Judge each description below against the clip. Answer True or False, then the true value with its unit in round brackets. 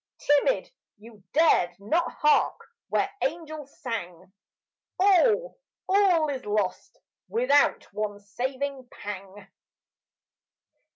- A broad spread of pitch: True (8.2 semitones)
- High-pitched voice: True (270 Hz)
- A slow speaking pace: True (90 wpm)